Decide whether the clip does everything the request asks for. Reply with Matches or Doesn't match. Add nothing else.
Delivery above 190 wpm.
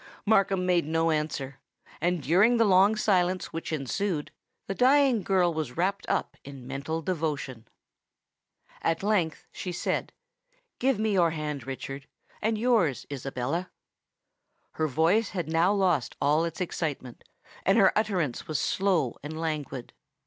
Doesn't match